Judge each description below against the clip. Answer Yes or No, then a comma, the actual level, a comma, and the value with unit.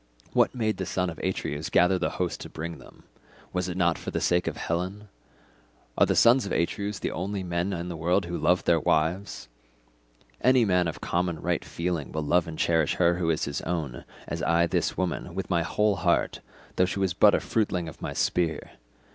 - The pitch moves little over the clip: Yes, narrow, 2.1 semitones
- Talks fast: Yes, fast, 210 wpm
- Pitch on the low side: Yes, very low, 90 Hz